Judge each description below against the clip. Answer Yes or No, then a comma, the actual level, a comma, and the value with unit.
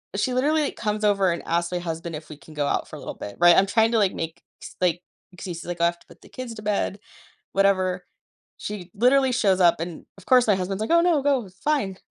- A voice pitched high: Yes, high, 195 Hz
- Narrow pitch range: No, average, 4.9 semitones